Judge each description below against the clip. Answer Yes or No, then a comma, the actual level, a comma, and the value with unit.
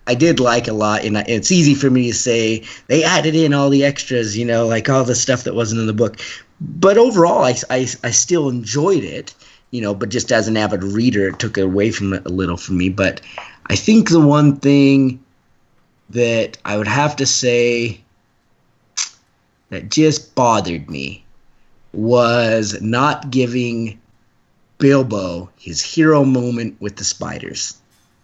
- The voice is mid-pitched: No, low, 120 Hz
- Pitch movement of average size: Yes, average, 4.5 semitones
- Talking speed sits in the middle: Yes, average, 170 wpm